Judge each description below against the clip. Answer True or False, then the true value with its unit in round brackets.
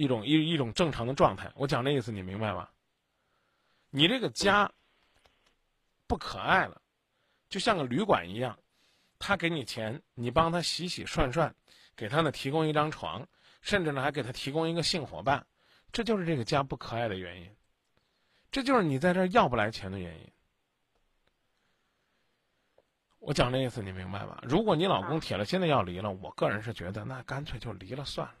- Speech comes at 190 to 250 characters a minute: False (265 characters per minute)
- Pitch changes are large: True (7.0 semitones)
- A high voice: False (140 Hz)